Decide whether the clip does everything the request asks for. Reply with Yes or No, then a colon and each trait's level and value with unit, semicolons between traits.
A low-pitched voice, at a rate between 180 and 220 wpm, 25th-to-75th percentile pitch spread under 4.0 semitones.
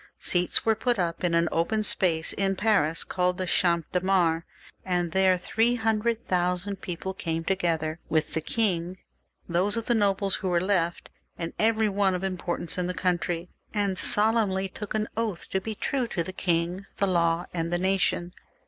No: medium, 185 Hz; average, 185 wpm; average, 2.9 semitones